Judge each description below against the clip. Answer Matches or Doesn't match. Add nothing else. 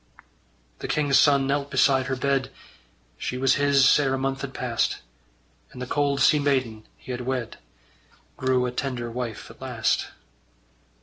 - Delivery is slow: Doesn't match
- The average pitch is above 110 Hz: Matches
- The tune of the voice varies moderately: Doesn't match